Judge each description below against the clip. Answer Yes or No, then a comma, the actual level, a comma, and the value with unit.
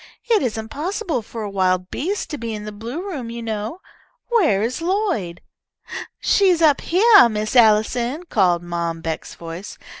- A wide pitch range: Yes, wide, 8.6 semitones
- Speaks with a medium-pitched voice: No, high, 230 Hz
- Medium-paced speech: Yes, average, 160 wpm